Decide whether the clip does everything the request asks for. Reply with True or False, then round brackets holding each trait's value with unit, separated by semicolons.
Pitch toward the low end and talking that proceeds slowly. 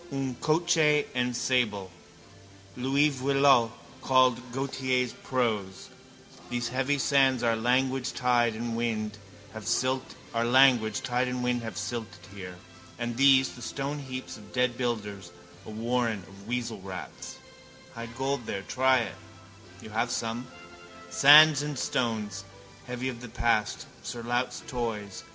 True (125 Hz; 115 wpm)